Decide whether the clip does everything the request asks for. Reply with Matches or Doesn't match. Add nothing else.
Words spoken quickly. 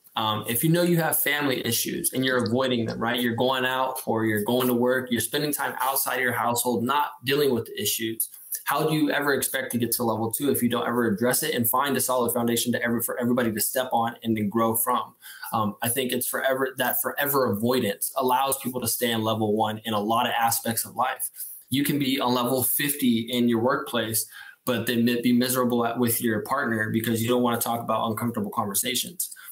Matches